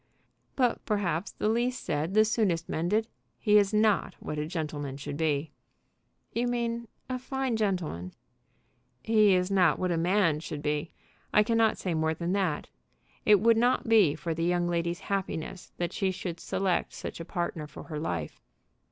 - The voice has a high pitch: No, medium, 180 Hz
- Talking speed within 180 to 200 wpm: No, average, 170 wpm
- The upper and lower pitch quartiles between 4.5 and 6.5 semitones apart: Yes, average, 5.1 semitones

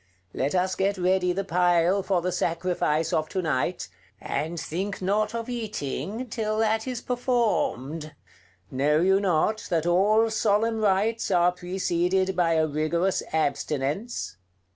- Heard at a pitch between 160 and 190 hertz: Yes, medium, 185 Hz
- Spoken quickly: No, average, 140 wpm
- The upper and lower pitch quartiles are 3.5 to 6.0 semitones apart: Yes, average, 4.4 semitones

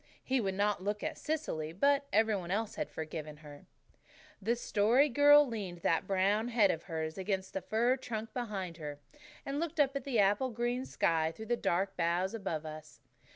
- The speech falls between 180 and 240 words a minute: Yes, average, 190 wpm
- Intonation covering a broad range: Yes, wide, 5.9 semitones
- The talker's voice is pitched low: No, high, 205 Hz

